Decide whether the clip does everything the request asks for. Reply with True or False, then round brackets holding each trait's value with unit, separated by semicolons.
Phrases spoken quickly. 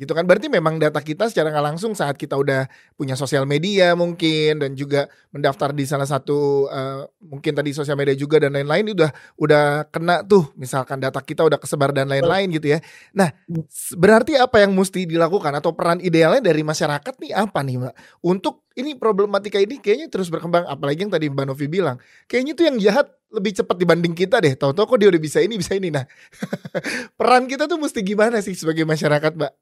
True (200 wpm)